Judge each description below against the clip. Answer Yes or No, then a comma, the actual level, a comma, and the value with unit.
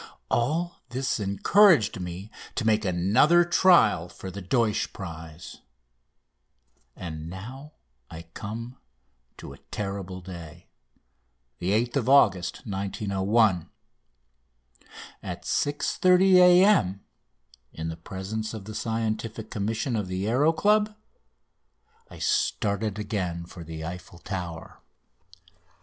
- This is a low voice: Yes, low, 105 Hz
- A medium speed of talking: No, slow, 100 wpm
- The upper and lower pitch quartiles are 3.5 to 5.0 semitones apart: No, wide, 5.4 semitones